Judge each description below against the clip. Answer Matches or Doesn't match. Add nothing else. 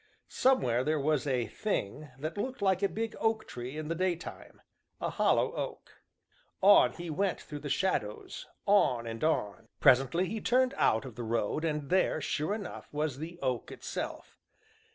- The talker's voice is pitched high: Doesn't match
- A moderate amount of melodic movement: Doesn't match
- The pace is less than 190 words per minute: Matches